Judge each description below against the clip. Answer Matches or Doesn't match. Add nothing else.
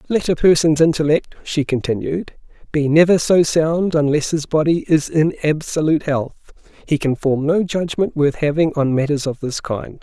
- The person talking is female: Doesn't match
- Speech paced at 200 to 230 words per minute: Doesn't match